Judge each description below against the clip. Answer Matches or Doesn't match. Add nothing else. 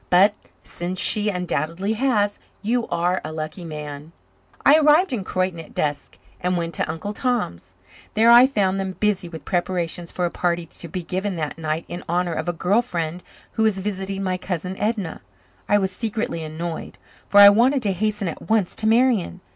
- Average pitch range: Matches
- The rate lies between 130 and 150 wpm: Doesn't match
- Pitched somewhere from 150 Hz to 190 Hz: Matches